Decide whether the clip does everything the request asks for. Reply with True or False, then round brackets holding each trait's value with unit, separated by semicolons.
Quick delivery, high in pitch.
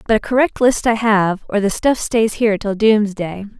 True (215 wpm; 215 Hz)